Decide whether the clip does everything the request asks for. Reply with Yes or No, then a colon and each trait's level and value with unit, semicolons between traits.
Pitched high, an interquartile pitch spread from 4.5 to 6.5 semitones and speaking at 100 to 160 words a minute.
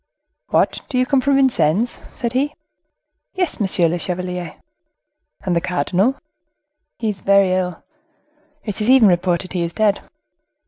Yes: high, 195 Hz; wide, 5.5 semitones; average, 140 wpm